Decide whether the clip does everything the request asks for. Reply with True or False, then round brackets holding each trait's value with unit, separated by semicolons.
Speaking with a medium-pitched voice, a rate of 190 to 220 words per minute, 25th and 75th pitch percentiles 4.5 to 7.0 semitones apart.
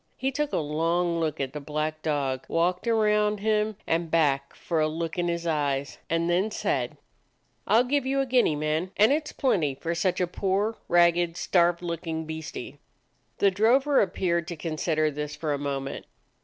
True (170 Hz; 195 wpm; 4.9 semitones)